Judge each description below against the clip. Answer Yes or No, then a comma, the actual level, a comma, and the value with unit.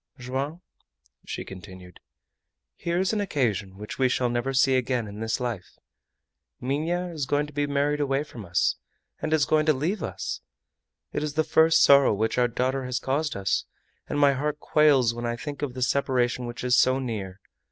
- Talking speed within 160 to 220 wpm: Yes, average, 190 wpm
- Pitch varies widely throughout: No, average, 3.6 semitones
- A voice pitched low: Yes, low, 130 Hz